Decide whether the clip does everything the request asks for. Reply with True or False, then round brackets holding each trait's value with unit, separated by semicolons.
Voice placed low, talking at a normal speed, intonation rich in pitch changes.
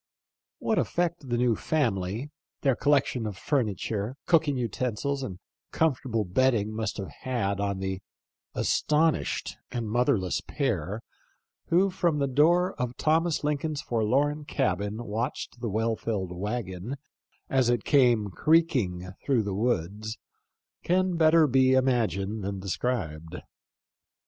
False (120 Hz; 125 wpm; 6.0 semitones)